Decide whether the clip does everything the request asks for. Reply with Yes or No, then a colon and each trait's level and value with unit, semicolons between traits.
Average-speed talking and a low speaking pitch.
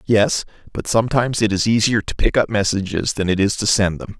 No: fast, 230 wpm; low, 105 Hz